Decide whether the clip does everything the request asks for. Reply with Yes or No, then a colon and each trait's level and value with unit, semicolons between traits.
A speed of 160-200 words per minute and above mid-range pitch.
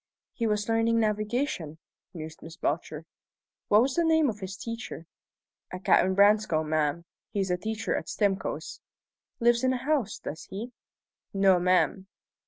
No: average, 150 wpm; high, 205 Hz